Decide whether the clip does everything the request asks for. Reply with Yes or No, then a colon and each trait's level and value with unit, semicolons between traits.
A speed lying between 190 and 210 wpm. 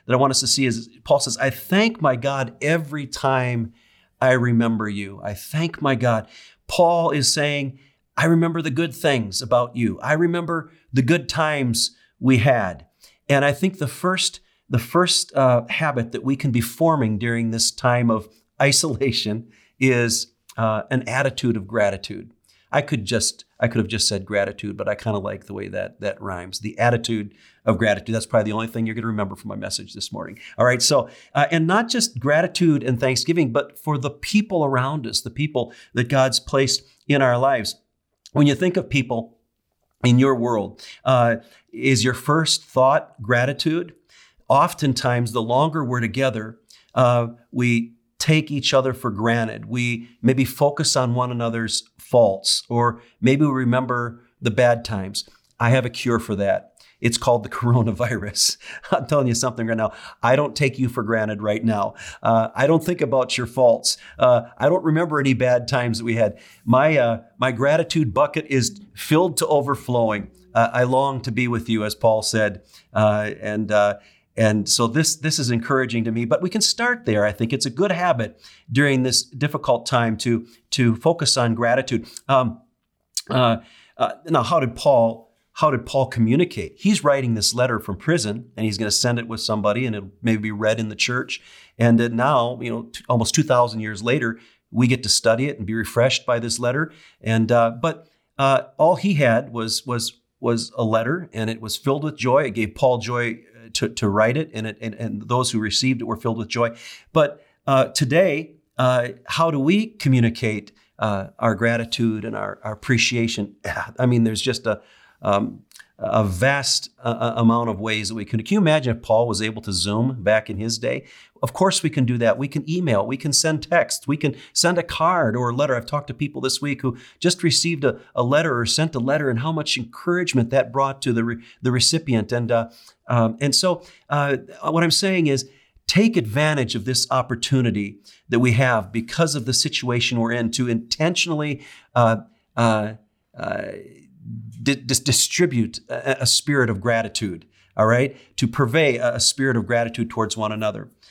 Yes: average, 195 wpm